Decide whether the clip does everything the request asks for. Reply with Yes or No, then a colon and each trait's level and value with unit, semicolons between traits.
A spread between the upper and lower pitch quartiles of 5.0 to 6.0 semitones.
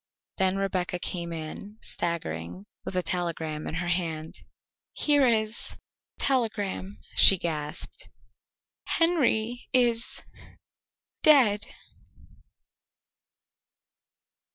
Yes: wide, 5.5 semitones